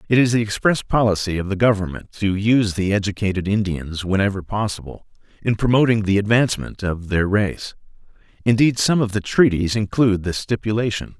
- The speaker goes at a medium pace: Yes, average, 160 wpm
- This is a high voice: No, low, 105 Hz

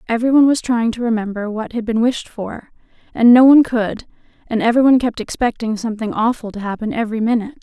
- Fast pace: No, average, 190 wpm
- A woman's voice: Yes, female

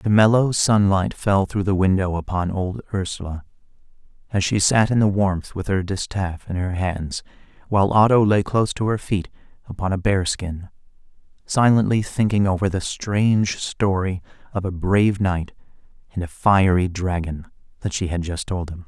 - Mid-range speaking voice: No, very low, 95 Hz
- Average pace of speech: Yes, average, 170 wpm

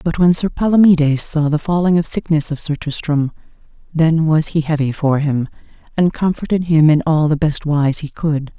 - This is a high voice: No, medium, 155 Hz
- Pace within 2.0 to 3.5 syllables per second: No, 5.0 syllables/s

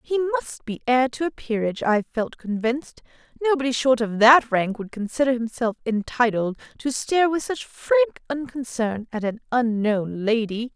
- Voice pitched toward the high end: Yes, very high, 250 Hz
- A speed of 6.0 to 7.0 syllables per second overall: No, 5.5 syllables/s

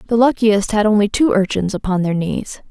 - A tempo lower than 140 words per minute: No, average, 200 wpm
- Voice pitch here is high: Yes, high, 205 Hz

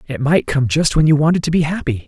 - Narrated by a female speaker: No, male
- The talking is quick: Yes, fast, 290 wpm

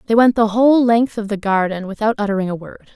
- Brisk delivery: Yes, fast, 245 wpm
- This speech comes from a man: No, female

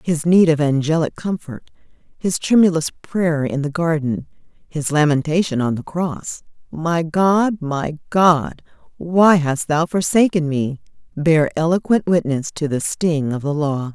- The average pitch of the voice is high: No, medium, 160 Hz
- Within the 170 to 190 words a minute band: No, average, 145 wpm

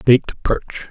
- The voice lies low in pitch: Yes, low, 120 Hz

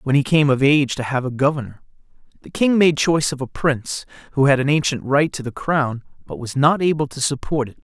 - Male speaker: Yes, male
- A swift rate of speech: Yes, fast, 235 wpm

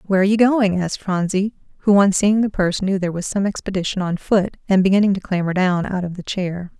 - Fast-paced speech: Yes, fast, 230 wpm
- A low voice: No, high, 190 Hz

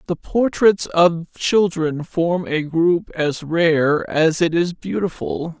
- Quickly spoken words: No, average, 140 wpm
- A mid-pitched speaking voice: Yes, medium, 170 Hz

